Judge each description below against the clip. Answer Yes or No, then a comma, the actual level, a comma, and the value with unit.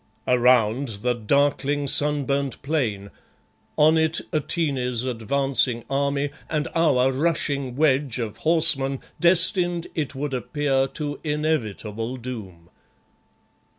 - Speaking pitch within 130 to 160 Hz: Yes, medium, 140 Hz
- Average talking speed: No, slow, 100 wpm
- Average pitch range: Yes, average, 3.2 semitones